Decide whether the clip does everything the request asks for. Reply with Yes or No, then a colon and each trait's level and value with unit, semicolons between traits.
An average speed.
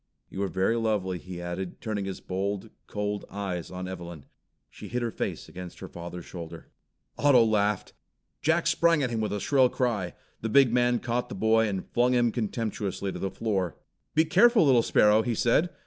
Yes: average, 190 wpm